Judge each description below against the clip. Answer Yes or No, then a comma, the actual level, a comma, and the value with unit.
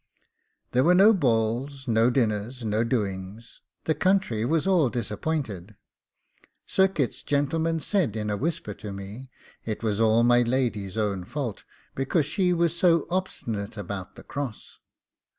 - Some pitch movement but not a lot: No, wide, 6.8 semitones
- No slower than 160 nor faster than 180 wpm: No, average, 145 wpm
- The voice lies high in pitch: No, low, 120 Hz